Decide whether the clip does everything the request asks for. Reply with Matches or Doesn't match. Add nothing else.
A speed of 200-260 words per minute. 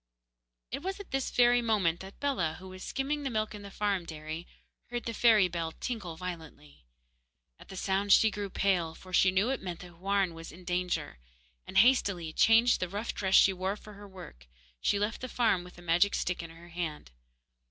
Matches